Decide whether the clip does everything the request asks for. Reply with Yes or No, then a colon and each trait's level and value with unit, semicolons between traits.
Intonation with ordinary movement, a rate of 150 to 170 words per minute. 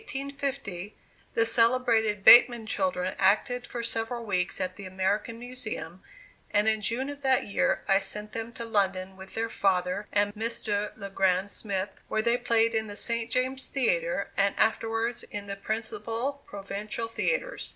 Yes: average, 3.3 semitones; average, 160 wpm